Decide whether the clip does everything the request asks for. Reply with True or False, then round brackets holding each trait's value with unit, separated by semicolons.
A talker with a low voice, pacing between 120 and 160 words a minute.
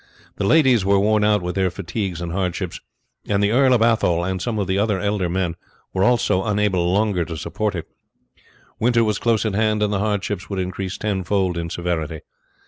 False (100 Hz; 205 wpm)